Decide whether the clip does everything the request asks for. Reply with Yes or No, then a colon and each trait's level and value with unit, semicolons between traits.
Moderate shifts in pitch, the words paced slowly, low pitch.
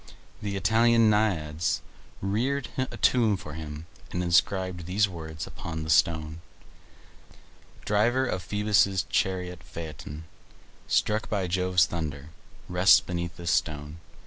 Yes: average, 4.5 semitones; slow, 120 wpm; very low, 90 Hz